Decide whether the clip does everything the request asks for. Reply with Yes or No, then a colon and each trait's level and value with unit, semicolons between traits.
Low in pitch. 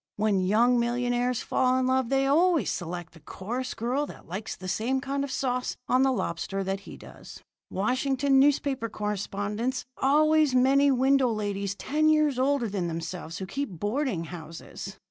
No: high, 245 Hz